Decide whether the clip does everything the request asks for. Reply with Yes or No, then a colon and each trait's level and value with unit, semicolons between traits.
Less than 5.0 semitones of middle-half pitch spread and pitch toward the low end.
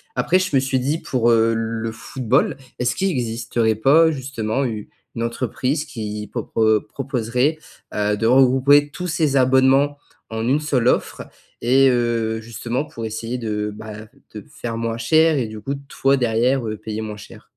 Yes: average, 3.4 semitones; low, 120 Hz